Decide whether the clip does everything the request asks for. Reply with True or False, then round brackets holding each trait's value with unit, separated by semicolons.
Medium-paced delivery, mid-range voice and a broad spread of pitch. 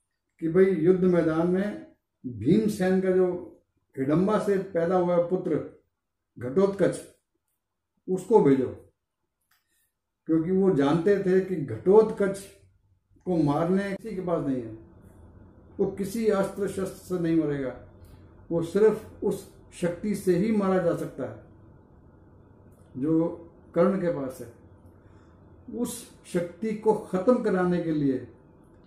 True (125 wpm; 170 Hz; 7.3 semitones)